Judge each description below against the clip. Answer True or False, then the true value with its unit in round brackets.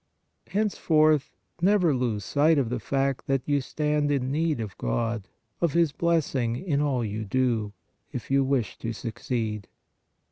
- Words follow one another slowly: False (150 wpm)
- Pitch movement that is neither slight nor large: True (4.7 semitones)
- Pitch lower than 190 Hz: True (135 Hz)